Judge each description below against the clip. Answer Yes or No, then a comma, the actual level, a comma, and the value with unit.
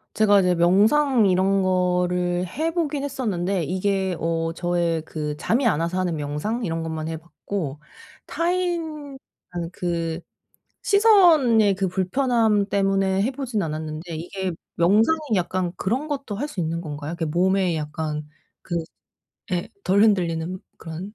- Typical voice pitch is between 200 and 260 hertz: No, medium, 185 Hz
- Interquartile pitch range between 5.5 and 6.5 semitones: No, average, 5.1 semitones